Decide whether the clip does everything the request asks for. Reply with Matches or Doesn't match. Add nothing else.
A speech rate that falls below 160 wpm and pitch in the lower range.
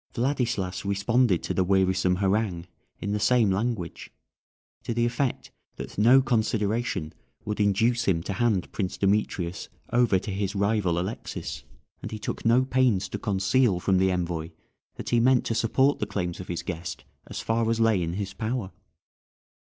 Doesn't match